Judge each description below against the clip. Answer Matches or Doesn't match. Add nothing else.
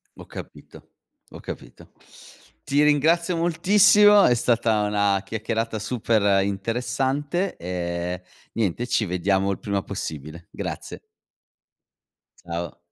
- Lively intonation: Matches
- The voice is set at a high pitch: Doesn't match